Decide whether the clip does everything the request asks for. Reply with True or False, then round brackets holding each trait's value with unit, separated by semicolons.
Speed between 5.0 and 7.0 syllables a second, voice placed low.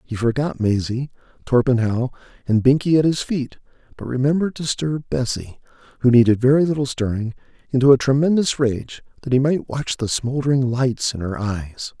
True (5.2 syllables/s; 130 Hz)